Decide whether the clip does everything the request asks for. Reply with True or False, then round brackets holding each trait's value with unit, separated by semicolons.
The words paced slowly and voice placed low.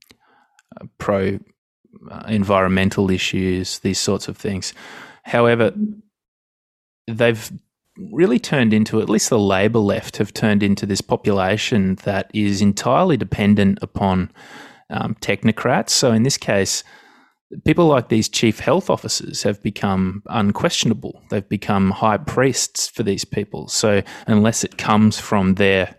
True (130 wpm; 105 Hz)